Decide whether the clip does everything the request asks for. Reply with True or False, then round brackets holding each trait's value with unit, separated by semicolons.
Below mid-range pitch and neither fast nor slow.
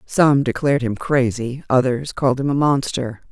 True (130 Hz; 165 wpm)